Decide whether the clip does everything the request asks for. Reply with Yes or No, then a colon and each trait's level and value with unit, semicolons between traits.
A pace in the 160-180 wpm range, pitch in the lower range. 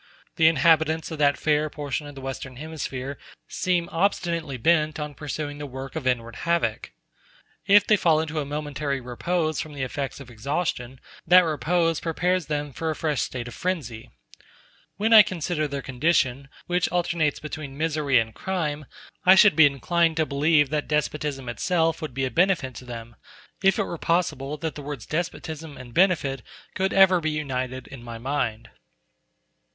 No: average, 170 wpm; medium, 150 Hz